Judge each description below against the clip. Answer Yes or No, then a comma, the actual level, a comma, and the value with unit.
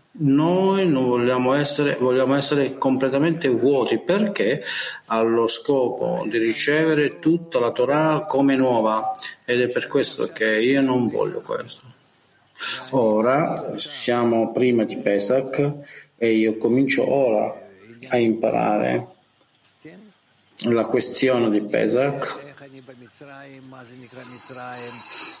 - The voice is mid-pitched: No, low, 130 Hz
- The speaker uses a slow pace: Yes, slow, 100 wpm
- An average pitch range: Yes, average, 3.4 semitones